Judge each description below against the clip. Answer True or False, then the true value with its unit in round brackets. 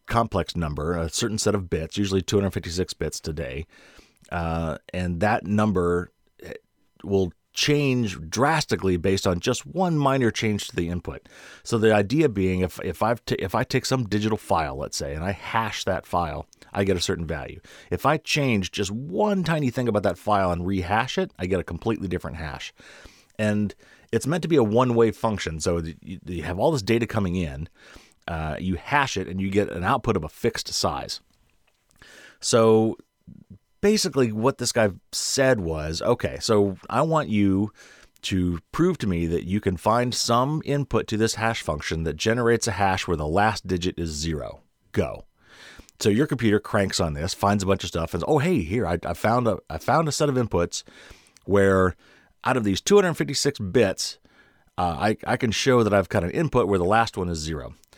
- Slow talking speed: False (195 wpm)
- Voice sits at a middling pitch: False (100 Hz)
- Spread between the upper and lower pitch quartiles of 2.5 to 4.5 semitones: False (5.1 semitones)